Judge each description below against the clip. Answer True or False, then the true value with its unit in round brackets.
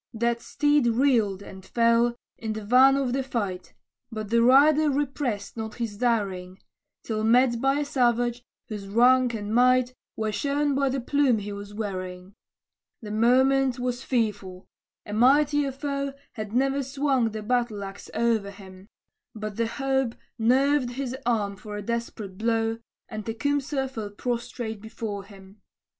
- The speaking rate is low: False (150 wpm)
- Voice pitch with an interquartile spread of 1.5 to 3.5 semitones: False (4.0 semitones)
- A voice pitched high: True (235 Hz)